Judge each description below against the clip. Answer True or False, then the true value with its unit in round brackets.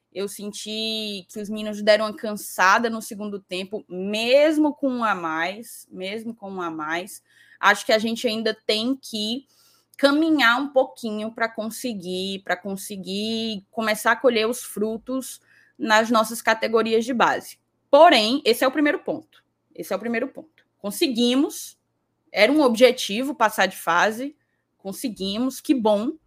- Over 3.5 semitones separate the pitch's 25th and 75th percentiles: True (4.0 semitones)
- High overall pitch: True (225 Hz)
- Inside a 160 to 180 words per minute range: False (150 wpm)